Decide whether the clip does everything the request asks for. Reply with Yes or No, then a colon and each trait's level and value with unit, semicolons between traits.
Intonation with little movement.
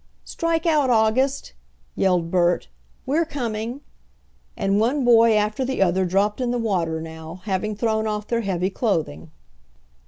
No: average, 4.8 semitones